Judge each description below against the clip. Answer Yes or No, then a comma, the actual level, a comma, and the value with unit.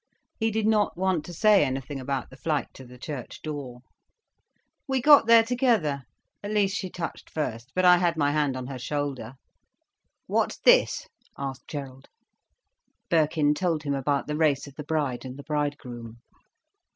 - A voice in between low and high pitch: Yes, medium, 150 Hz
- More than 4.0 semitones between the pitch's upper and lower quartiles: Yes, average, 5.1 semitones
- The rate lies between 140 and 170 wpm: Yes, average, 165 wpm